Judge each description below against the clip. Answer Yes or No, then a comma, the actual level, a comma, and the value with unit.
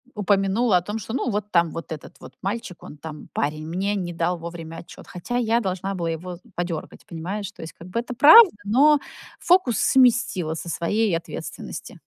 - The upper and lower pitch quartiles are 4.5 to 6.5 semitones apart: Yes, average, 5.0 semitones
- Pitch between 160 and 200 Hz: Yes, high, 190 Hz